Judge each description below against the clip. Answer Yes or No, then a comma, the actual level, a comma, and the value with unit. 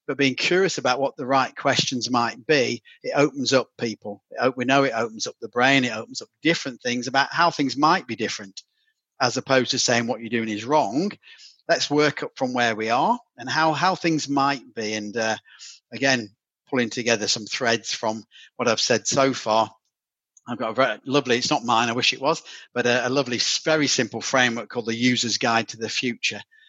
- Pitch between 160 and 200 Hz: No, low, 125 Hz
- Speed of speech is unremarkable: No, fast, 210 wpm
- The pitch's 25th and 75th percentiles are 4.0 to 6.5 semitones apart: No, average, 3.3 semitones